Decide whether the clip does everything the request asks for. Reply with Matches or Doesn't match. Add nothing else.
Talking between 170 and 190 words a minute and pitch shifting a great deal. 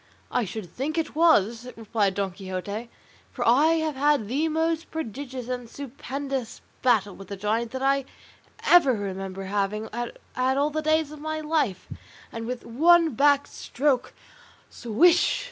Doesn't match